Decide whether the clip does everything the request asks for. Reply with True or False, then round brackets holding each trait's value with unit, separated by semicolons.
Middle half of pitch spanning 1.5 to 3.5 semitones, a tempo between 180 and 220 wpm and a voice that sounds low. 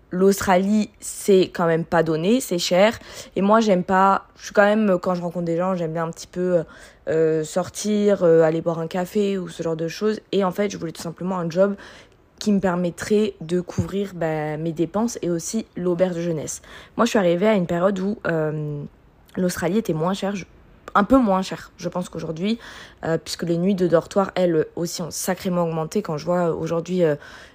False (3.0 semitones; 205 wpm; 180 Hz)